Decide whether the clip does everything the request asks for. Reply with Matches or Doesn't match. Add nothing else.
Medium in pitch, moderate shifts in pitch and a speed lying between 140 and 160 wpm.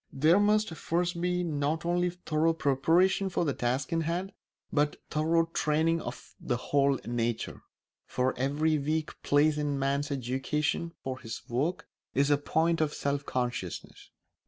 Matches